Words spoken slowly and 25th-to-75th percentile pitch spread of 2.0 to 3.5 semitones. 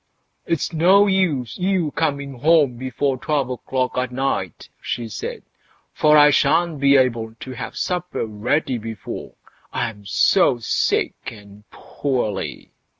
No: slow, 125 wpm; average, 5.1 semitones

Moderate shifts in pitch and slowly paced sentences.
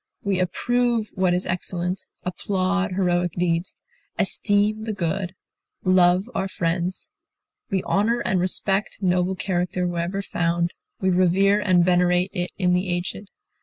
No: narrow, 1.9 semitones; slow, 130 wpm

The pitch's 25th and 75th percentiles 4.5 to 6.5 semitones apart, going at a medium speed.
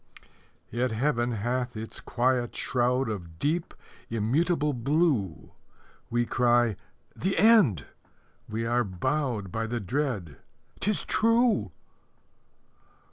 No: average, 5.0 semitones; slow, 100 wpm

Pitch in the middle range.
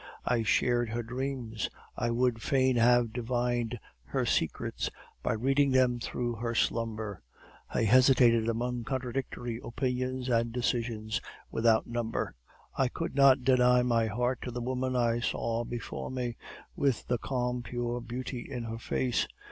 No: low, 120 Hz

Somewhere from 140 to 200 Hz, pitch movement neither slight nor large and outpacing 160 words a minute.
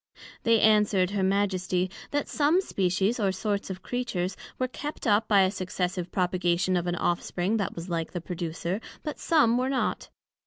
Yes: high, 190 Hz; average, 4.0 semitones; average, 170 wpm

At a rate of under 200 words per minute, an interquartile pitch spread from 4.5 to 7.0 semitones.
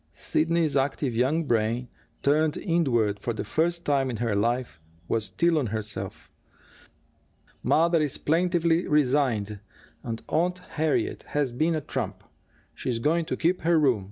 Yes: average, 145 wpm; wide, 5.6 semitones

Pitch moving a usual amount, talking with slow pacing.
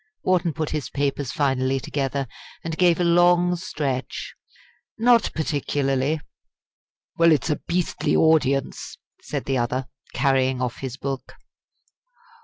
Yes: average, 3.8 semitones; slow, 120 wpm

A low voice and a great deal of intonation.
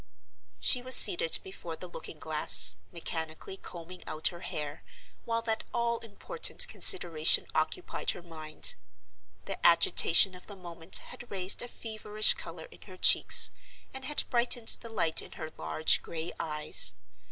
No: medium, 185 Hz; wide, 6.4 semitones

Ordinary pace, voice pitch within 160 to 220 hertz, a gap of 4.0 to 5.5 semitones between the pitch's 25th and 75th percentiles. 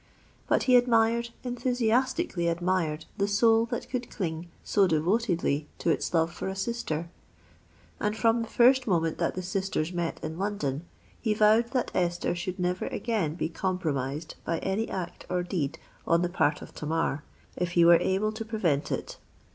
Yes: average, 165 wpm; medium, 185 Hz; average, 5.1 semitones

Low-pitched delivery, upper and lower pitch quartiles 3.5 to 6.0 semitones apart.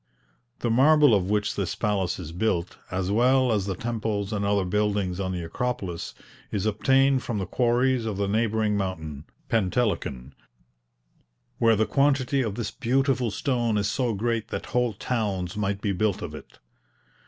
Yes: low, 105 Hz; average, 3.8 semitones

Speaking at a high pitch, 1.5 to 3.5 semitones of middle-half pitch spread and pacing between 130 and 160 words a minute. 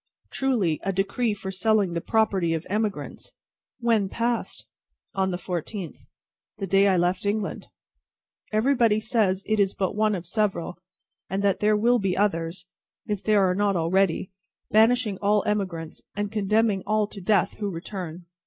Yes: high, 200 Hz; narrow, 2.6 semitones; average, 155 wpm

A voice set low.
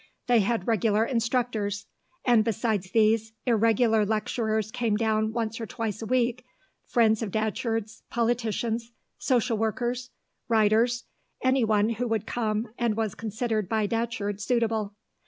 No: high, 225 Hz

